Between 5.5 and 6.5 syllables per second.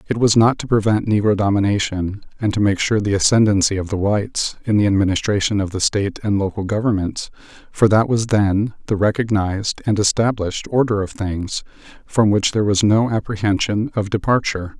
Yes: 5.6 syllables/s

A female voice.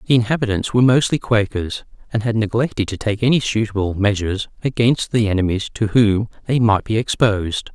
No: male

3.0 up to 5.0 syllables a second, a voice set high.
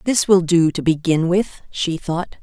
No: 4.5 syllables/s; medium, 175 Hz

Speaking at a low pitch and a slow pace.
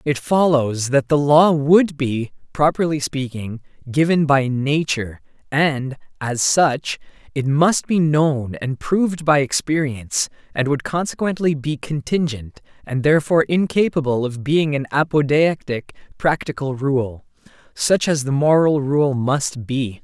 No: medium, 145 Hz; slow, 130 wpm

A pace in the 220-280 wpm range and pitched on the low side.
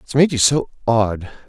No: fast, 205 wpm; low, 120 Hz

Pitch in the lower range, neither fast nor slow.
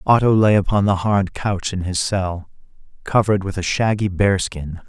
Yes: very low, 95 Hz; average, 185 wpm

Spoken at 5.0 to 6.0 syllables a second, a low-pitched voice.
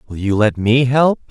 No: 4.7 syllables/s; low, 120 Hz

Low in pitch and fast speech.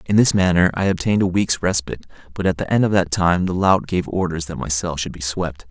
Yes: very low, 90 Hz; fast, 265 wpm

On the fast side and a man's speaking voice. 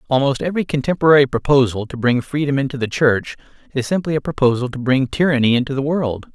No: average, 190 wpm; male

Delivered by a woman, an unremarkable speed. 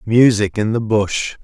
No: male; average, 165 wpm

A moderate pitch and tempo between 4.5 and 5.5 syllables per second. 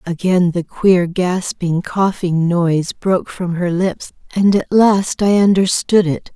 No: medium, 180 Hz; 3.9 syllables/s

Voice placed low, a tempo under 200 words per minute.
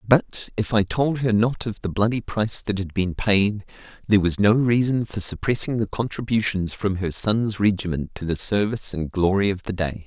No: low, 105 Hz; fast, 205 wpm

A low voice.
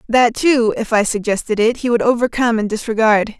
No: high, 225 Hz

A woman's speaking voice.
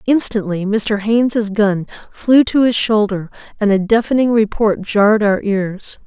Yes: female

